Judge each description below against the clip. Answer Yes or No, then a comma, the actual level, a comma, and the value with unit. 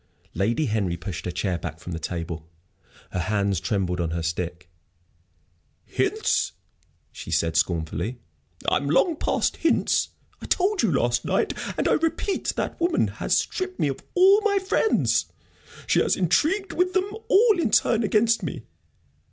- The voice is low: Yes, low, 120 Hz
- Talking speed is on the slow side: No, average, 155 wpm